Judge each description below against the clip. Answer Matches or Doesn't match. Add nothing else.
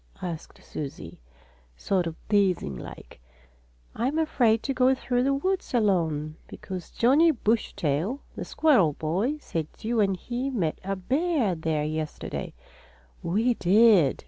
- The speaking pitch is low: Doesn't match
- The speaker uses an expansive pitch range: Matches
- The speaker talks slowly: Matches